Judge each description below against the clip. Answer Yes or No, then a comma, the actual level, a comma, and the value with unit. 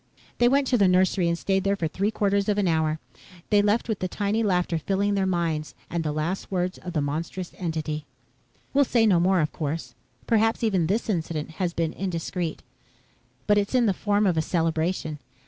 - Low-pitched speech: No, medium, 185 Hz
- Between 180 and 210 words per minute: Yes, average, 200 wpm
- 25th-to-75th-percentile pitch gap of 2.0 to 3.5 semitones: No, average, 3.9 semitones